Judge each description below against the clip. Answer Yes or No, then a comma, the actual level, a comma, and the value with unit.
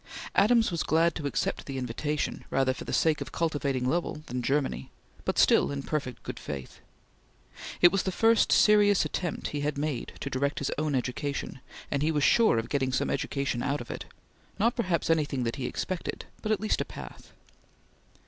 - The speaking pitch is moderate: Yes, medium, 145 Hz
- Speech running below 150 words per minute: No, average, 190 wpm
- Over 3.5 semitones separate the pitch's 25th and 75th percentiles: Yes, average, 4.3 semitones